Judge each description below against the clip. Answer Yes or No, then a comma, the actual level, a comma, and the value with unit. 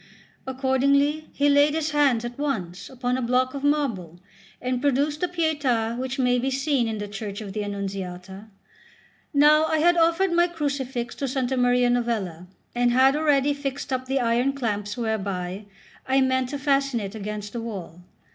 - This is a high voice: Yes, very high, 255 Hz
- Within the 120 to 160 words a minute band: No, average, 175 wpm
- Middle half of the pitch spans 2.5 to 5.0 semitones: Yes, average, 4.5 semitones